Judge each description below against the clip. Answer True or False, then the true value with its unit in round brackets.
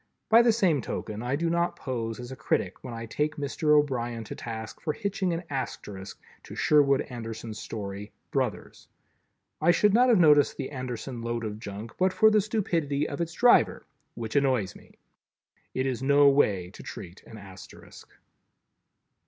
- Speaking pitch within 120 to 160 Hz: True (135 Hz)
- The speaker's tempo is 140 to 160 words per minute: False (170 wpm)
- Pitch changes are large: True (6.6 semitones)